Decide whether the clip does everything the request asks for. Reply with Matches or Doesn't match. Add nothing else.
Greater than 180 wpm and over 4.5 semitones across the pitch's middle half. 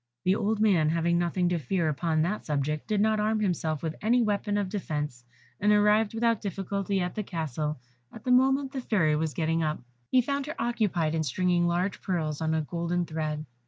Matches